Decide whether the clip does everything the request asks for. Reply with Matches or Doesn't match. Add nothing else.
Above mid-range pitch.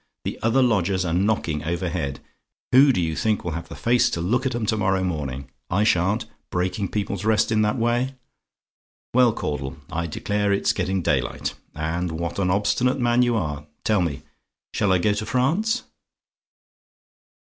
Doesn't match